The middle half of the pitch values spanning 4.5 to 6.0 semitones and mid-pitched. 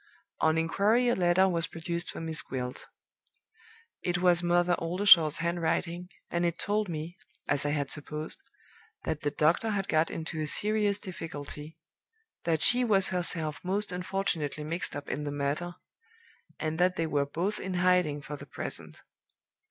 No: average, 3.0 semitones; medium, 170 Hz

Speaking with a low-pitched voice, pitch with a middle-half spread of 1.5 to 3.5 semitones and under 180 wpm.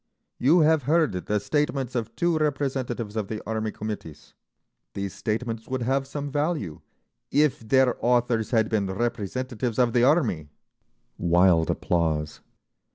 No: low, 120 Hz; average, 4.7 semitones; slow, 135 wpm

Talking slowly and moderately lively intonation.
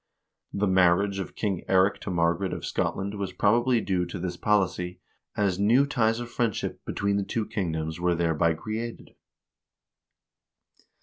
No: average, 150 wpm; average, 3.4 semitones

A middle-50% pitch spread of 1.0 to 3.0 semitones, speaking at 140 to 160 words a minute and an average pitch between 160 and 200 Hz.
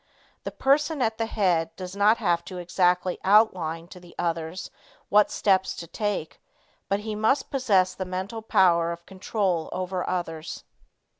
No: average, 3.4 semitones; average, 155 wpm; medium, 185 Hz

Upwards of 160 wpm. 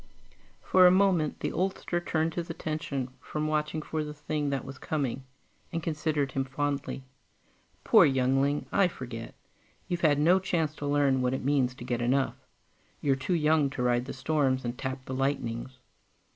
Yes: average, 170 wpm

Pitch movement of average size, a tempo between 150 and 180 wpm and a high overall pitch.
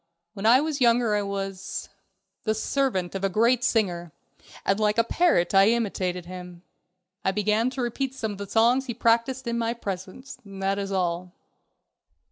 Yes: average, 3.6 semitones; average, 170 wpm; high, 215 Hz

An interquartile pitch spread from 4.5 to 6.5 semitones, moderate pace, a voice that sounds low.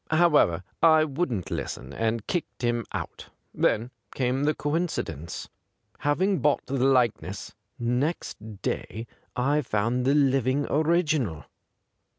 No: average, 4.9 semitones; slow, 115 wpm; low, 130 Hz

